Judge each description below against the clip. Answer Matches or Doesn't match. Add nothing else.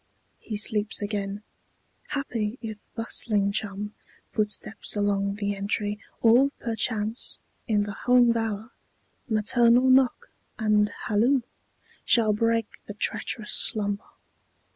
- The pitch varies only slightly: Matches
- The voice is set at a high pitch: Matches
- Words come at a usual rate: Doesn't match